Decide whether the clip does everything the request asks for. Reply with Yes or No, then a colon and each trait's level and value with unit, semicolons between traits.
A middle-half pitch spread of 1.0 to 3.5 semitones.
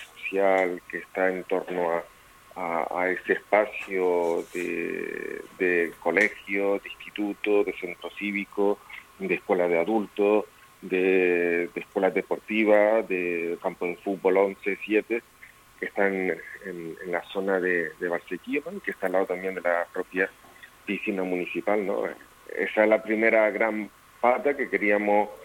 Yes: narrow, 2.6 semitones